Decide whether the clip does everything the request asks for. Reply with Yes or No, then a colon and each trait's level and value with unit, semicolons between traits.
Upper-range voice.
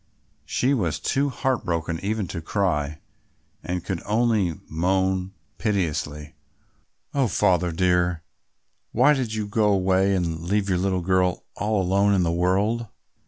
No: very low, 95 Hz